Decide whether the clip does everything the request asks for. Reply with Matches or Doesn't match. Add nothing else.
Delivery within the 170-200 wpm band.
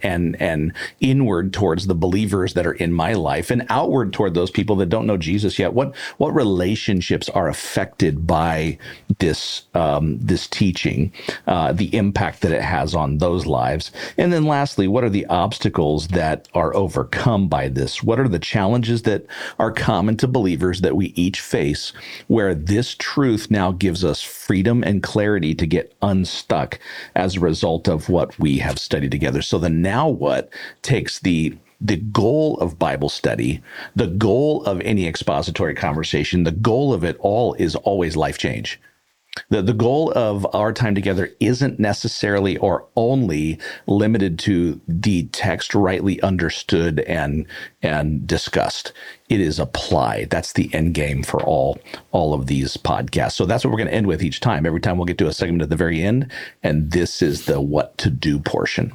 Matches